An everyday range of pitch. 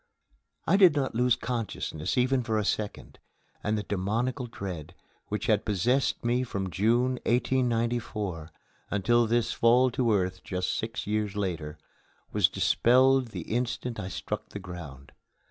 Yes: average, 4.2 semitones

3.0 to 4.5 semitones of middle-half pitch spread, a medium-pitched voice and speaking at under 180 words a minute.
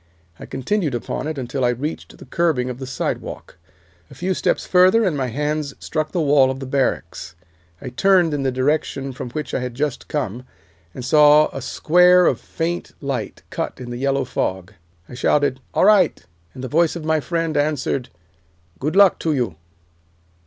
No: average, 3.9 semitones; medium, 145 Hz; average, 185 wpm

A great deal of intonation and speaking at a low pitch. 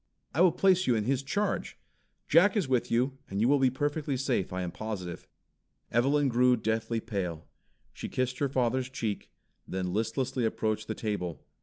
No: average, 4.1 semitones; low, 125 Hz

